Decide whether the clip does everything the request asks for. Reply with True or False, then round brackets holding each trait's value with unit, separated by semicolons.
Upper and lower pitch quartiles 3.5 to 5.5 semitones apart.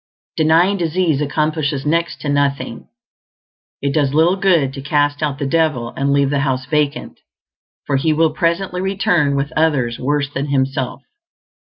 False (2.7 semitones)